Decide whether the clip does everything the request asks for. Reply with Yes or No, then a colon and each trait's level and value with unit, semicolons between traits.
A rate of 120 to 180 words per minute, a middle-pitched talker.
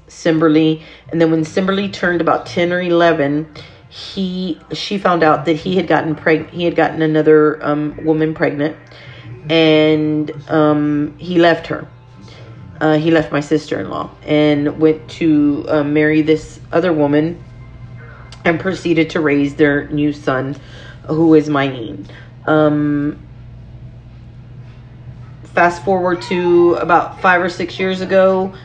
Yes: average, 140 wpm; medium, 155 Hz